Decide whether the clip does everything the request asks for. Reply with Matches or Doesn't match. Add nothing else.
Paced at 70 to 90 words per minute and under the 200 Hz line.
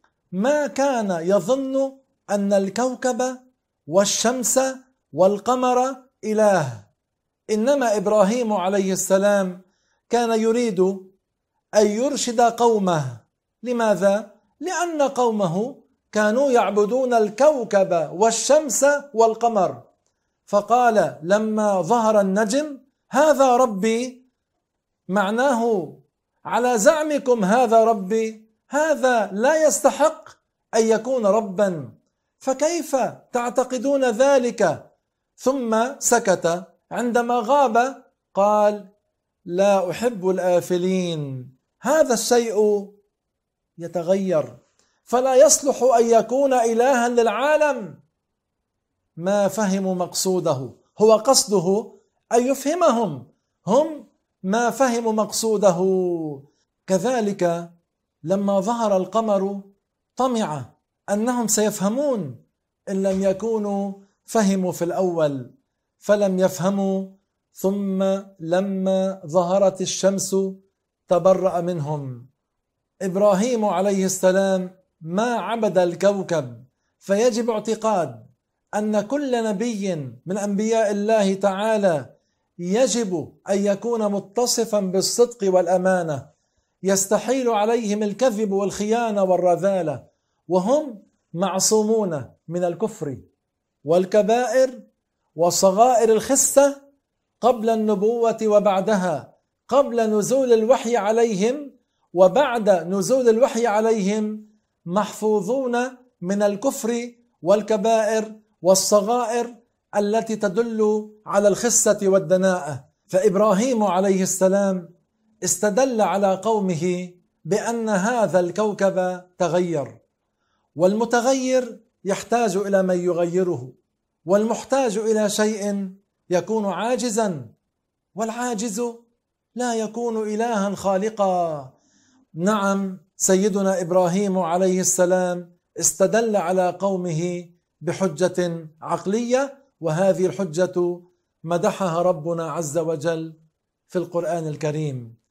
Doesn't match